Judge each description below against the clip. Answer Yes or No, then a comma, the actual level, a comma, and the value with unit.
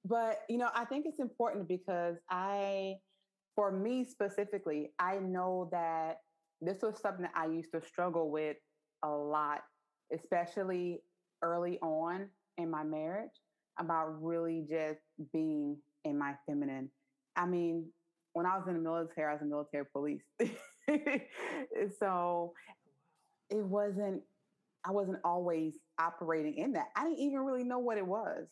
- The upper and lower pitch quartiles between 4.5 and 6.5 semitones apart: No, average, 4.1 semitones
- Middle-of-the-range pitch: Yes, medium, 175 Hz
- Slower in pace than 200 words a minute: Yes, average, 145 wpm